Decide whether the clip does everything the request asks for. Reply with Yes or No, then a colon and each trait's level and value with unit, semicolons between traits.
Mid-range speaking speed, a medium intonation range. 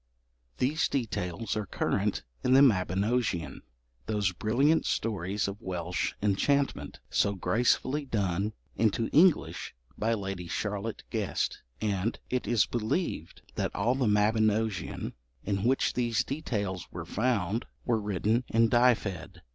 No: slow, 125 wpm; average, 3.8 semitones